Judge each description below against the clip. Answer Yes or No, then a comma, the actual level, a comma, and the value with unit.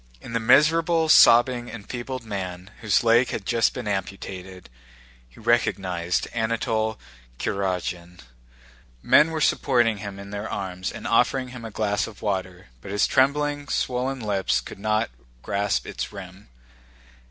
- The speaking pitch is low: Yes, low, 110 Hz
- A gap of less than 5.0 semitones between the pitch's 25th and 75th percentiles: Yes, average, 4.0 semitones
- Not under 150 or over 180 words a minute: No, average, 140 wpm